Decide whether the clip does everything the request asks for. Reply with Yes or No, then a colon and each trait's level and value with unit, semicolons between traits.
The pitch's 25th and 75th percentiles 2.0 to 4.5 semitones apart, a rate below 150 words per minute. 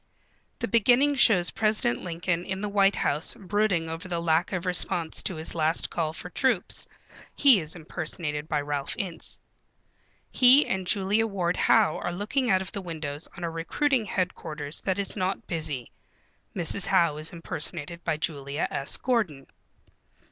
No: average, 4.1 semitones; average, 160 wpm